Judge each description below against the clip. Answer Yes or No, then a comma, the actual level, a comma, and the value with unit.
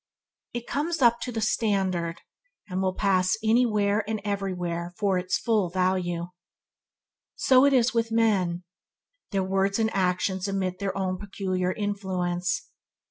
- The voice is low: No, high, 195 Hz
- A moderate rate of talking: No, slow, 130 wpm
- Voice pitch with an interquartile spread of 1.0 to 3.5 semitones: Yes, average, 3.1 semitones